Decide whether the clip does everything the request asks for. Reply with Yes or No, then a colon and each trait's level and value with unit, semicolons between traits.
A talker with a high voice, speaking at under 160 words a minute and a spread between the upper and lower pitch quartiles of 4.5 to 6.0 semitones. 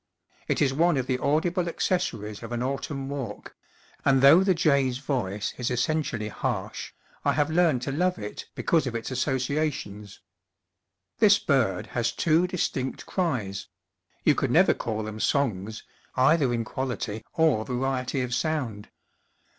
No: low, 130 Hz; average, 150 wpm; average, 5.1 semitones